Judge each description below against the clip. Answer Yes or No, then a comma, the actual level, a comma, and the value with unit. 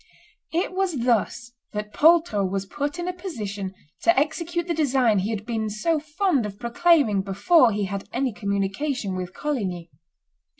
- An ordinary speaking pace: Yes, average, 160 wpm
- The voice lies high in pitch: Yes, high, 240 Hz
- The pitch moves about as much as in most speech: No, wide, 8.1 semitones